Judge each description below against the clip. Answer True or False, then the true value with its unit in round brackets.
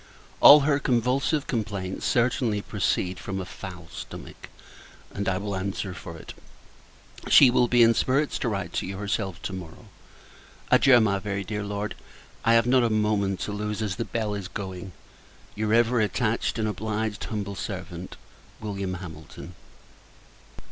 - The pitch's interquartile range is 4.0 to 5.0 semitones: False (3.2 semitones)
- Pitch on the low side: True (105 Hz)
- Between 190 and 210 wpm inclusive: False (155 wpm)